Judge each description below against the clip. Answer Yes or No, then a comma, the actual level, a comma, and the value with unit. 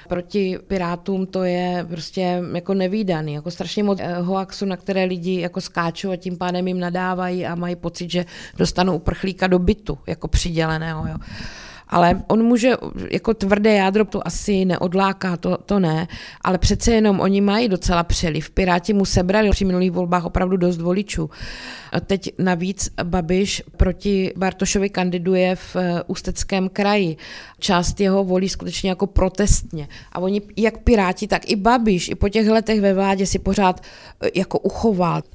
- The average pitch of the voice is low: No, medium, 185 Hz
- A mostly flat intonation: Yes, narrow, 1.9 semitones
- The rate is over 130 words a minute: Yes, average, 160 wpm